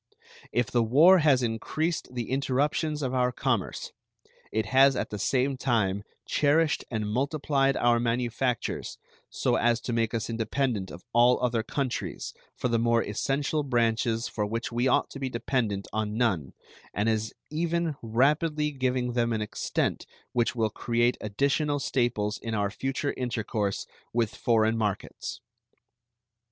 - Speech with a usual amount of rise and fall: Yes, average, 3.4 semitones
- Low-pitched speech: Yes, low, 120 Hz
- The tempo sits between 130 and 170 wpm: Yes, average, 145 wpm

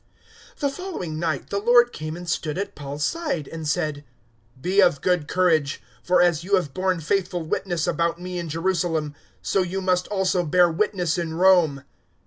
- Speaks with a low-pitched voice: No, medium, 175 Hz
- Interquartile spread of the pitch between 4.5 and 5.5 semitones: No, average, 3.0 semitones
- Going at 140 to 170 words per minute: No, average, 180 wpm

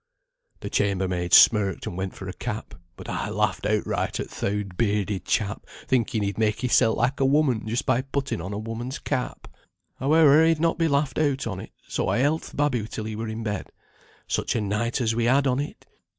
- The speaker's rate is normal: No, fast, 210 wpm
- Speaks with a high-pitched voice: No, low, 115 Hz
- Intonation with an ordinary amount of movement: Yes, average, 4.7 semitones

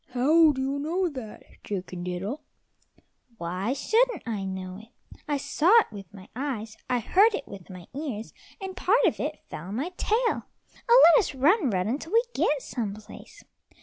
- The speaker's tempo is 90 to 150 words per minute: No, average, 180 wpm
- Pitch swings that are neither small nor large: No, wide, 8.5 semitones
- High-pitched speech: Yes, very high, 260 Hz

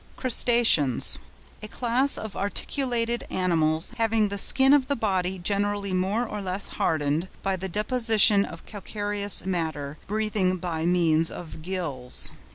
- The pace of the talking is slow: Yes, slow, 130 wpm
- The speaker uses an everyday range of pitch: Yes, average, 4.3 semitones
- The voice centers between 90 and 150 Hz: No, high, 195 Hz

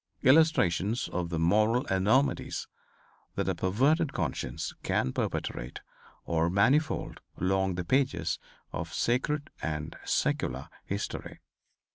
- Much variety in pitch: Yes, wide, 7.6 semitones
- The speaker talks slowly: Yes, slow, 105 wpm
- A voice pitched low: Yes, very low, 95 Hz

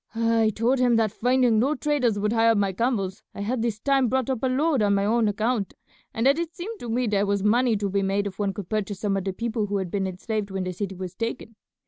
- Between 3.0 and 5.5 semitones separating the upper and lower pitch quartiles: Yes, average, 3.6 semitones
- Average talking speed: No, fast, 265 wpm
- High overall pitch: Yes, high, 220 Hz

